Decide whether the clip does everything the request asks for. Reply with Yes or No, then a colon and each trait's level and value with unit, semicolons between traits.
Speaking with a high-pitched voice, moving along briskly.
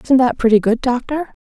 Yes: very high, 250 Hz; fast, 210 wpm